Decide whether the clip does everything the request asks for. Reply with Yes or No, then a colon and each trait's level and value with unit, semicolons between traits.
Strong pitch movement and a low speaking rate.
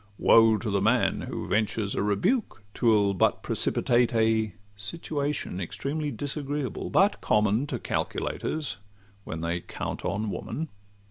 Yes: wide, 5.8 semitones; slow, 130 wpm